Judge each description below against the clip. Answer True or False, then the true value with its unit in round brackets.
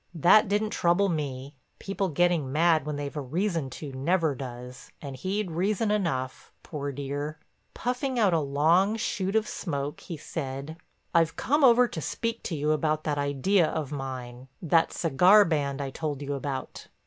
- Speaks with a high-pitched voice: False (155 Hz)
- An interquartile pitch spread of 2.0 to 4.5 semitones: False (5.2 semitones)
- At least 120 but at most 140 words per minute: False (165 wpm)